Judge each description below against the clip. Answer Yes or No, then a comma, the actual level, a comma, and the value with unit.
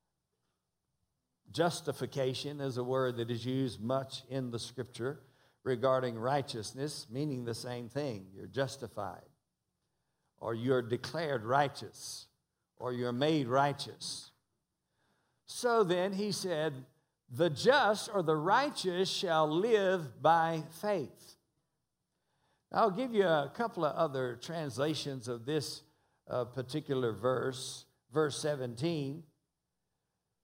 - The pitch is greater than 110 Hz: Yes, medium, 140 Hz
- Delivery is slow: Yes, slow, 110 wpm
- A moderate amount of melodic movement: Yes, average, 3.8 semitones